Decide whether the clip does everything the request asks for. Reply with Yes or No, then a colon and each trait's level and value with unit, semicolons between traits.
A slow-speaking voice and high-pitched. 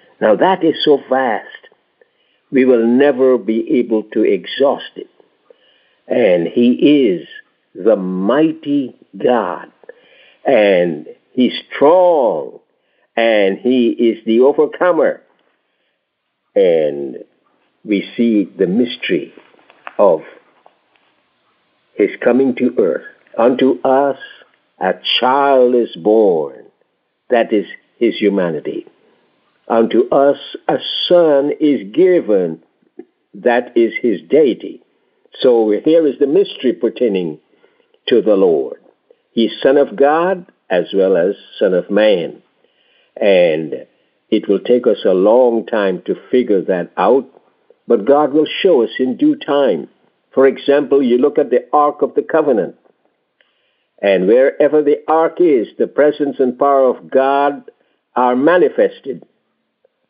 Yes: slow, 120 wpm; very high, 330 Hz